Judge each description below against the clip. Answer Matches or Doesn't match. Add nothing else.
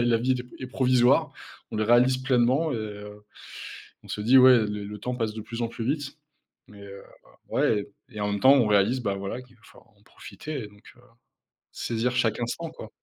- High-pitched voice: Doesn't match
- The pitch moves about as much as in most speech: Matches